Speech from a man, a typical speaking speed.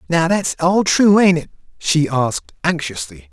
Yes: male; average, 165 wpm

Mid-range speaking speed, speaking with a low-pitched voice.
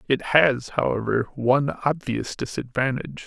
No: slow, 110 wpm; low, 130 Hz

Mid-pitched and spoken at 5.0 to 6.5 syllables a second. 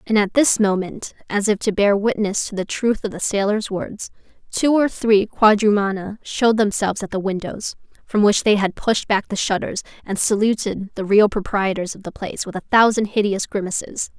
No: high, 205 Hz; 5.1 syllables/s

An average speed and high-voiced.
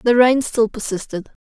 Yes: average, 165 wpm; high, 225 Hz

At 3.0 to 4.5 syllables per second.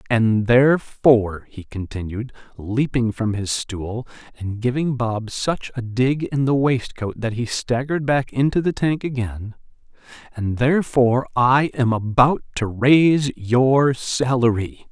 Yes: 4.1 syllables/s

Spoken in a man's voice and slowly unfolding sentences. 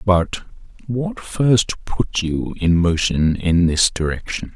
Yes: male; slow, 130 wpm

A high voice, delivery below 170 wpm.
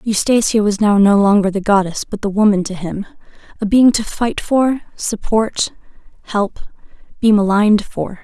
Yes: high, 210 Hz; average, 160 wpm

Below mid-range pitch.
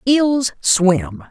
No: high, 200 Hz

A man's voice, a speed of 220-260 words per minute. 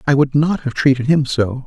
Yes: male; fast, 255 wpm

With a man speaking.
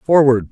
Yes: male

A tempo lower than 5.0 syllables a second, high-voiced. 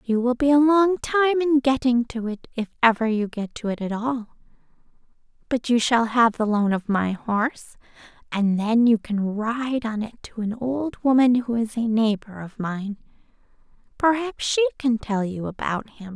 Yes: 4.6 syllables/s; high, 235 Hz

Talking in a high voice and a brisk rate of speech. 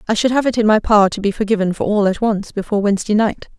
Yes: high, 210 Hz; fast, 285 wpm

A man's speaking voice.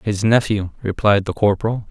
Yes: male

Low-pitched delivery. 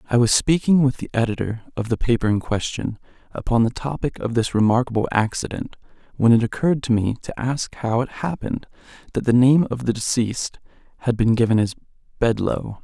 Yes: low, 120 Hz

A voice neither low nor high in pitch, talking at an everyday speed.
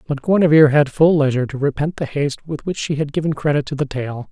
No: medium, 145 Hz; fast, 250 wpm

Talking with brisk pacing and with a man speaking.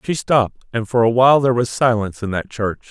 Yes: fast, 250 wpm; male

